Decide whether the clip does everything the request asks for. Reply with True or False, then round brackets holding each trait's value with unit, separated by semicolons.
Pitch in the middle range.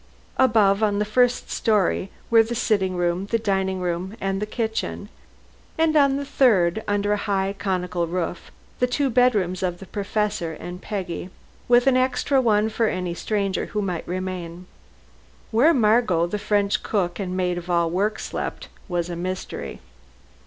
False (200 Hz)